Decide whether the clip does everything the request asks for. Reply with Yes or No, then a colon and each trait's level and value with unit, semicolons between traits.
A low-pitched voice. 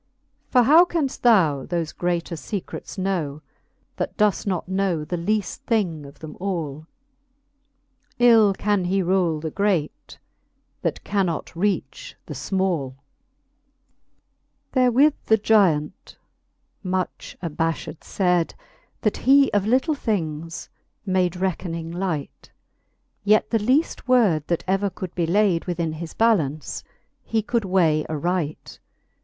No: medium, 185 Hz